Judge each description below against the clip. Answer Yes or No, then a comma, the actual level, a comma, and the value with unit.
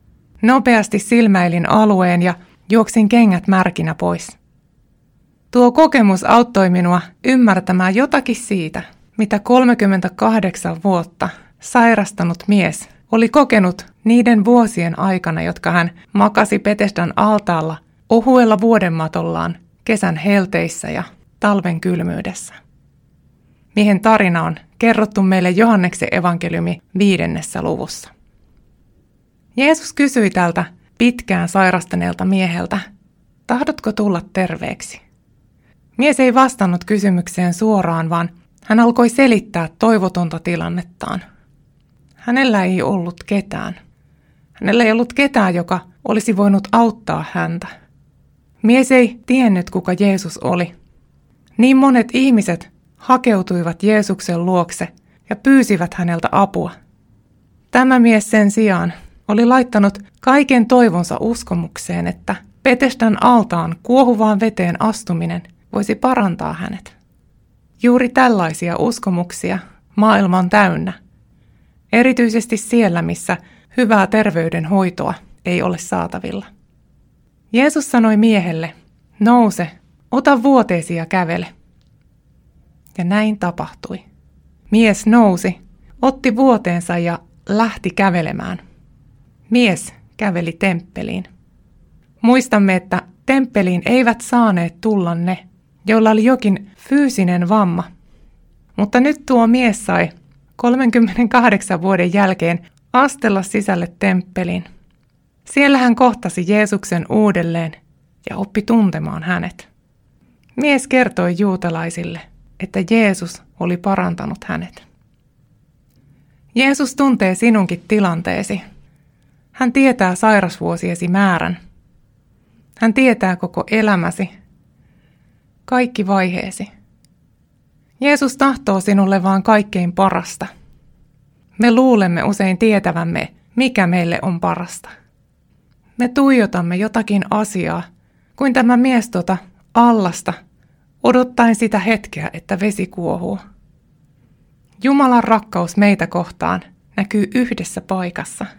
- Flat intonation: No, average, 4.7 semitones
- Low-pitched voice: No, high, 195 Hz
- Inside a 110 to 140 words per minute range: No, slow, 95 wpm